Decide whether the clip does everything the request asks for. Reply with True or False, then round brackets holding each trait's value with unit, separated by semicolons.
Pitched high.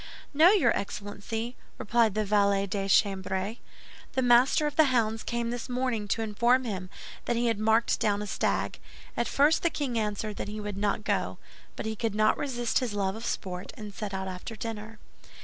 True (220 Hz)